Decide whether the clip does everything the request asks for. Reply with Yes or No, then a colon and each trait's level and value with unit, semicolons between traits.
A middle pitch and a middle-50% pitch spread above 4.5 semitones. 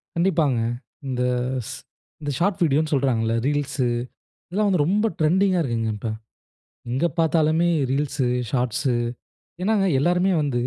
Yes: medium, 150 Hz; average, 5.1 semitones